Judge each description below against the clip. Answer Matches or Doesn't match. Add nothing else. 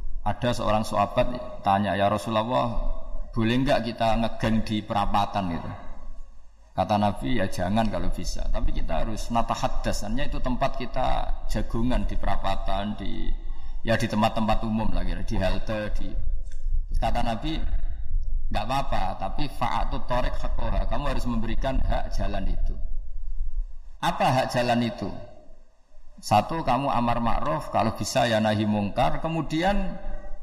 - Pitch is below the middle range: Matches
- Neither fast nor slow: Matches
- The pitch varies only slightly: Doesn't match